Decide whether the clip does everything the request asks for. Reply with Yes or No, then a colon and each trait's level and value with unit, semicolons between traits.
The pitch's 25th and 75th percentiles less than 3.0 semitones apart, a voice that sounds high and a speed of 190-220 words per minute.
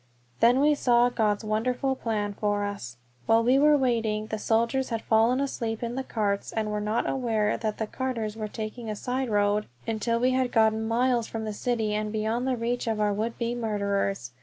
Yes: narrow, 2.4 semitones; high, 225 Hz; fast, 205 wpm